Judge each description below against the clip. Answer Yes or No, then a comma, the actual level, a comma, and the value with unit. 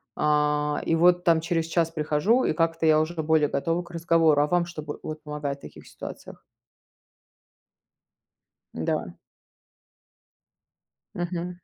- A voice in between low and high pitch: Yes, medium, 160 Hz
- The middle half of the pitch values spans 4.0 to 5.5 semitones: No, narrow, 2.4 semitones